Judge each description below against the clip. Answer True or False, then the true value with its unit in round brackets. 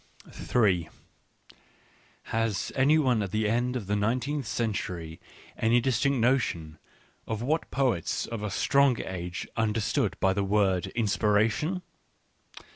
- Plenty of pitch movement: False (4.2 semitones)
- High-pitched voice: False (110 Hz)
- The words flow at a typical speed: False (120 wpm)